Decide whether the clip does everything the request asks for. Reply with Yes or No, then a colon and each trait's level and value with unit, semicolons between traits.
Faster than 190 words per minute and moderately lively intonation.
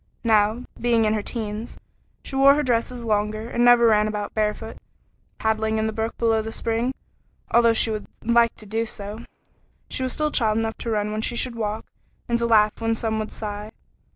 No: average, 200 wpm; narrow, 1.6 semitones